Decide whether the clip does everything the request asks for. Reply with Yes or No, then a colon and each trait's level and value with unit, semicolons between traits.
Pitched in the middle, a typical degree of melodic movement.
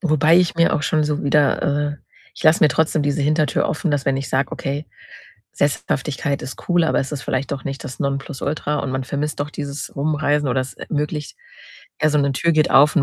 No: medium, 145 Hz; narrow, 1.9 semitones